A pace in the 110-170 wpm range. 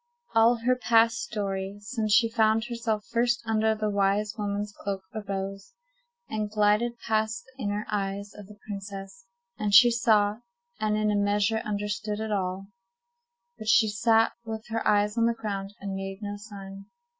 Yes: average, 165 wpm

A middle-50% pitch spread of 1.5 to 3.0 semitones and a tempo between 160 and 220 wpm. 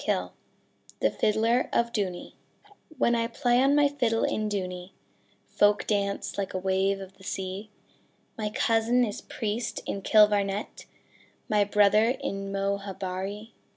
No: narrow, 2.4 semitones; slow, 135 wpm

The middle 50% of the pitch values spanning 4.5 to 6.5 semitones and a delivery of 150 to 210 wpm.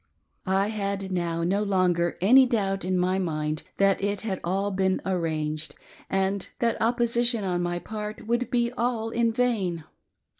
No: average, 4.1 semitones; average, 155 wpm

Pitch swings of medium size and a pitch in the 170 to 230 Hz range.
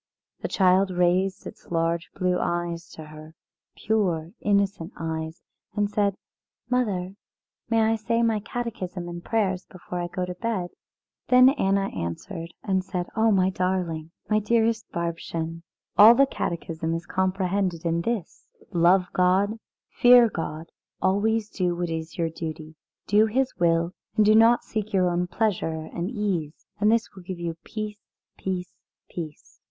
Yes: average, 3.8 semitones; medium, 185 Hz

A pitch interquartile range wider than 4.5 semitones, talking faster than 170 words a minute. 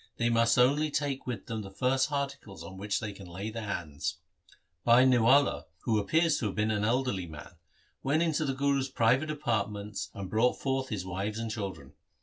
Yes: average, 5.0 semitones; average, 190 wpm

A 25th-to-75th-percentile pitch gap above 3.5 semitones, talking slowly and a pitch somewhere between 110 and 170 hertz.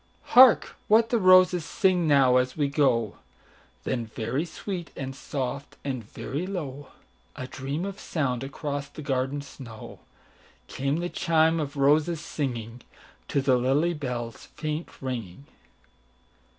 Yes: average, 4.1 semitones; slow, 120 wpm; medium, 140 Hz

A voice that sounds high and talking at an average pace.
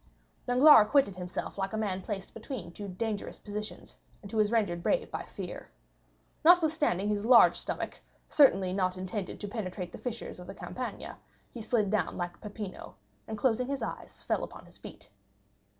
Yes: high, 210 Hz; average, 170 wpm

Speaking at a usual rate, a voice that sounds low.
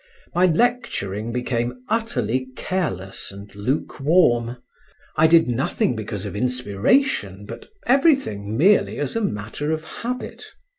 No: slow, 115 wpm; low, 125 Hz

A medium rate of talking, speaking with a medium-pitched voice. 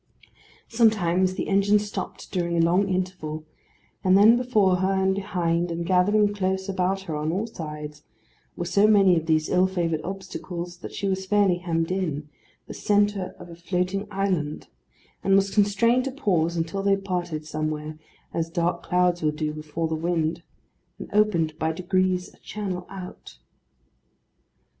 Yes: average, 160 wpm; medium, 180 Hz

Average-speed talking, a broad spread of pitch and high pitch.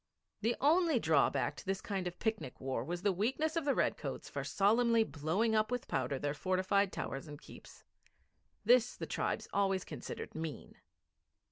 Yes: average, 165 wpm; wide, 6.4 semitones; high, 200 Hz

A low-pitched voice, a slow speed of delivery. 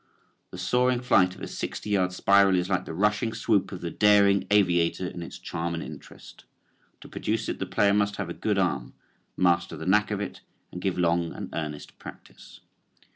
No: very low, 95 Hz; average, 195 wpm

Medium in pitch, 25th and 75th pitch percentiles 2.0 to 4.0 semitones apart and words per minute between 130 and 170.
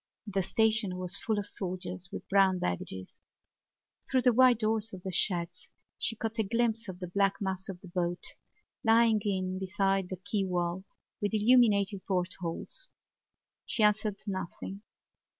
No: high, 195 Hz; average, 3.0 semitones; average, 150 wpm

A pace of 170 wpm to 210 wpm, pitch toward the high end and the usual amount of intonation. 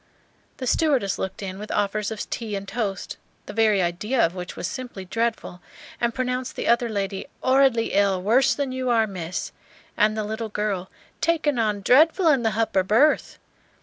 Yes: average, 180 wpm; high, 220 Hz; average, 4.2 semitones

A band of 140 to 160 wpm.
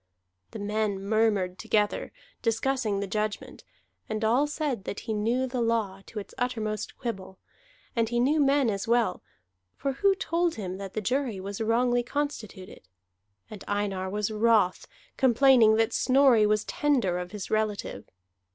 Yes: average, 150 wpm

